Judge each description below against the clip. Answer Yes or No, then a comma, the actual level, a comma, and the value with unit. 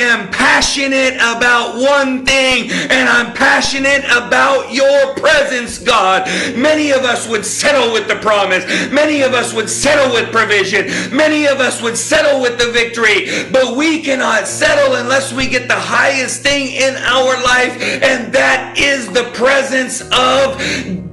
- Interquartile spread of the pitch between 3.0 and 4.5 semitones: No, narrow, 2.6 semitones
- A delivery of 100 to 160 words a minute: Yes, average, 155 wpm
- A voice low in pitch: No, very high, 260 Hz